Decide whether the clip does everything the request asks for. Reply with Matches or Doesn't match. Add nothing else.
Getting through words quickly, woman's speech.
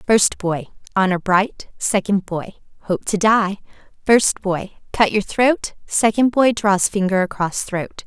Doesn't match